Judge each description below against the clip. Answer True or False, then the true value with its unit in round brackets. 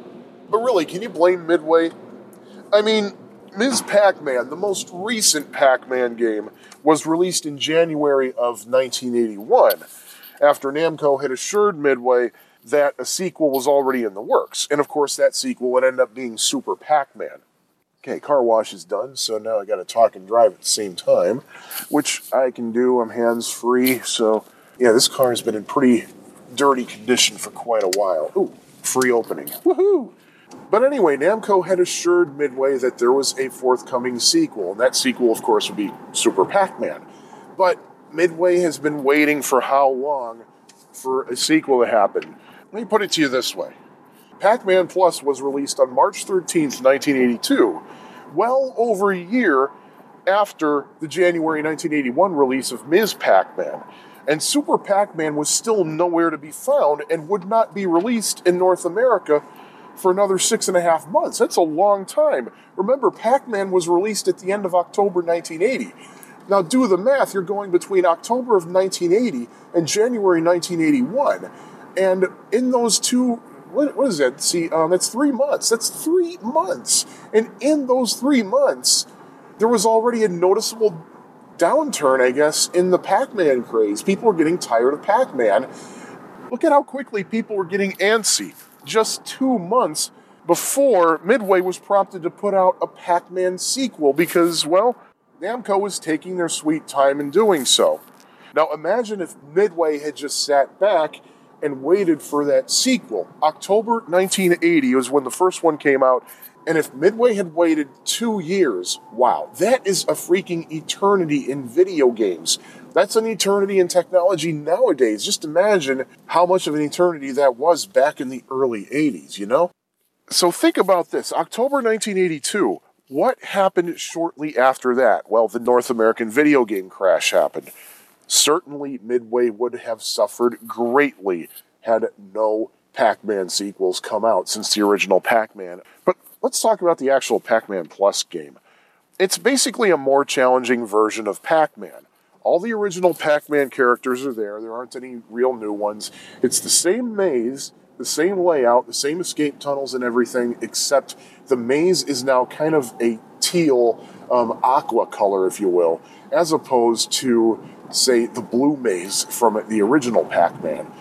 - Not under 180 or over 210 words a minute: False (165 wpm)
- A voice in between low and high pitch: True (175 Hz)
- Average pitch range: False (8.2 semitones)